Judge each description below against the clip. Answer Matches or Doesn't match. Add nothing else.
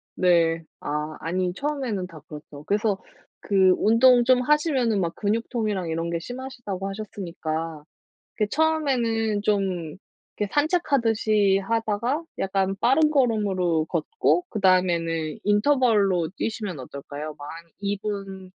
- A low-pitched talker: Doesn't match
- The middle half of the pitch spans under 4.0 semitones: Doesn't match